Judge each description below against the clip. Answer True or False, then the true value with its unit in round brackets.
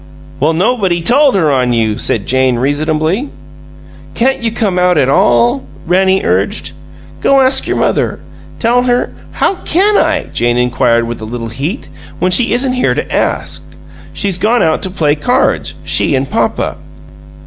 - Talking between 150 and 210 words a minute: True (165 wpm)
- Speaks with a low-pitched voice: False (180 Hz)